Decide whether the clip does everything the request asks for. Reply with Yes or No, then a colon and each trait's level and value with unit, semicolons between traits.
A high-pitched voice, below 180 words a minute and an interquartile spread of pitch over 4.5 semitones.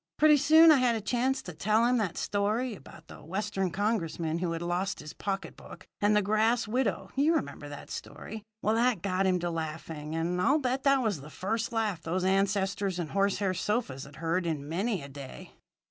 No: high, 195 Hz; fast, 205 wpm; average, 5.2 semitones